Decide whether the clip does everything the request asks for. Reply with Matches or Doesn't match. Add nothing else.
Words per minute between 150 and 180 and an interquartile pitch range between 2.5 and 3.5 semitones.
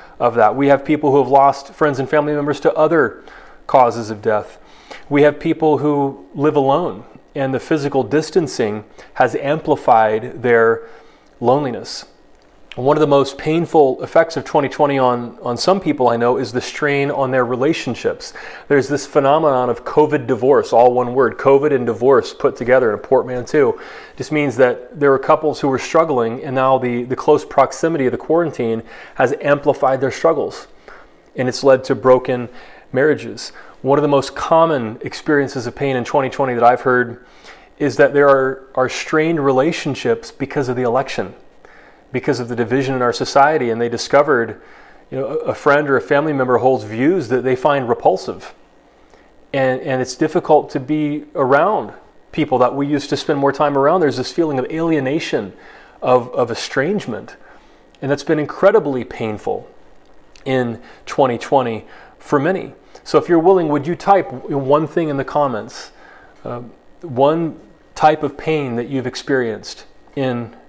Matches